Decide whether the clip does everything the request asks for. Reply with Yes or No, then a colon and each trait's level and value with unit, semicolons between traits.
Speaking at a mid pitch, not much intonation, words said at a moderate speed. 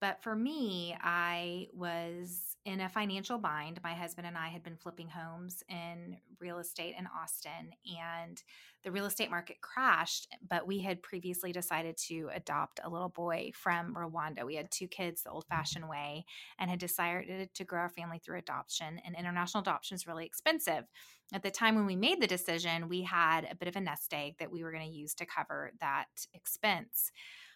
Yes: medium, 175 Hz; narrow, 1.9 semitones; average, 195 wpm